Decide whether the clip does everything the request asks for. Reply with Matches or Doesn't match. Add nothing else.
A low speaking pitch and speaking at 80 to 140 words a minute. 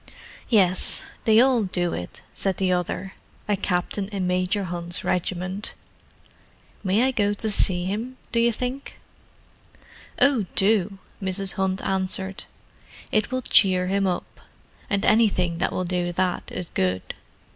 Doesn't match